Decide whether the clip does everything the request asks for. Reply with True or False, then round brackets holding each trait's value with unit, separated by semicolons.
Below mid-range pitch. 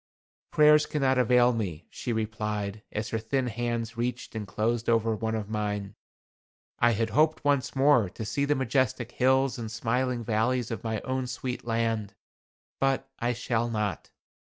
True (115 Hz)